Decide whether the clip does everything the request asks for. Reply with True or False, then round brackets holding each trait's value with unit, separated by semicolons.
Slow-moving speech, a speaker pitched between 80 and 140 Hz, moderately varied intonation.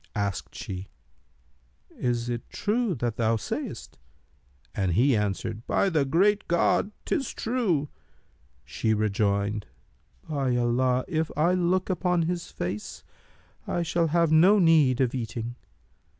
False (125 wpm; 135 Hz; 7.5 semitones)